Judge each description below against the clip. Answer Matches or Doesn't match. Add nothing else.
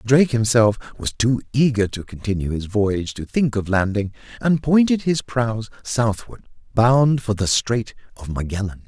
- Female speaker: Doesn't match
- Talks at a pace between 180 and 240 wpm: Doesn't match